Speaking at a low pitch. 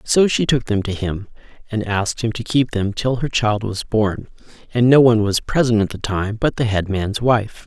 Yes: low, 110 Hz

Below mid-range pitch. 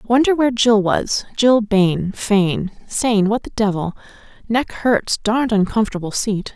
No: high, 215 Hz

